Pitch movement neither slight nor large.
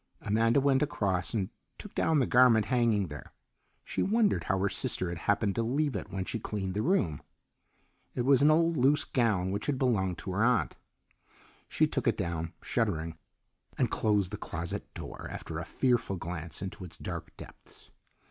No: wide, 5.9 semitones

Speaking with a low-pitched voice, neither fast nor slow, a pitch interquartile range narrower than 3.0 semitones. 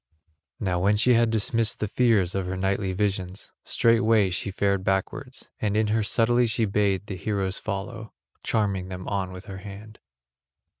Yes: low, 100 Hz; average, 165 wpm; narrow, 2.6 semitones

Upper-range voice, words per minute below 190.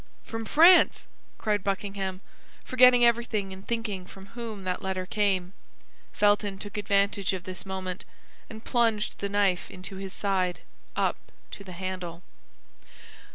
Yes: high, 200 Hz; slow, 135 wpm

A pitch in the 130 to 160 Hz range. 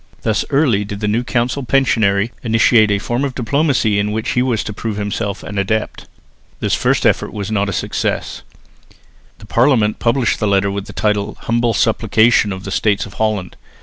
No: low, 110 Hz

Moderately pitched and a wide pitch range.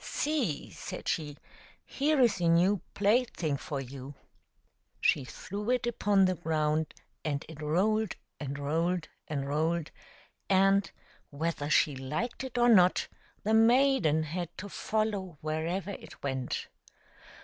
Yes: medium, 170 Hz; wide, 5.8 semitones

